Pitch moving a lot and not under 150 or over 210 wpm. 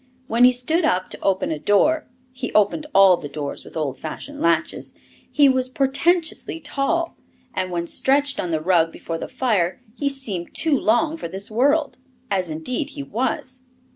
Yes: wide, 8.0 semitones; average, 175 wpm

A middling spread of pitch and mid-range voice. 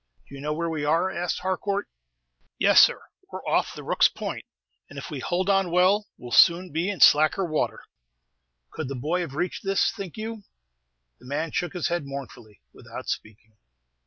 Yes: average, 4.6 semitones; medium, 170 Hz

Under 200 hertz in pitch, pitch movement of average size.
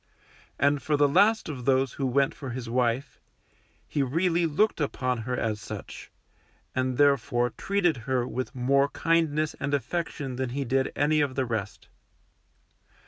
Yes: low, 135 Hz; average, 3.0 semitones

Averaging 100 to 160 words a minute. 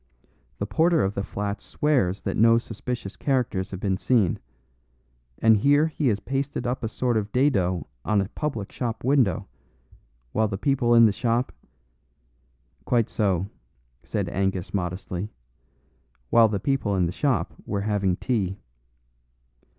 Yes: average, 150 wpm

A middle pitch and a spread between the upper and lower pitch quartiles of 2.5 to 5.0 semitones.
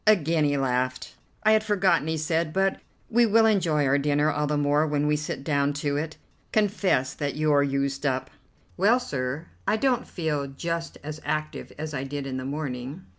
Yes: medium, 150 Hz; average, 3.2 semitones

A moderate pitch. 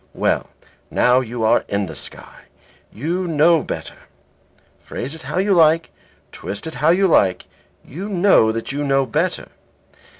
Yes: medium, 150 Hz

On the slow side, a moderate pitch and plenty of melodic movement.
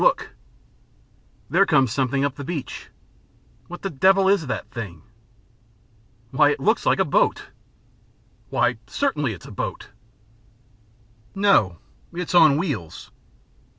Yes: slow, 120 wpm; medium, 150 Hz; wide, 6.6 semitones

